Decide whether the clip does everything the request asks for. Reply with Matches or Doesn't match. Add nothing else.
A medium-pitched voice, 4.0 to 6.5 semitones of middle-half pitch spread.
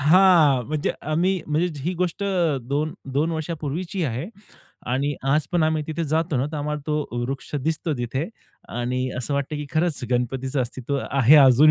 Doesn't match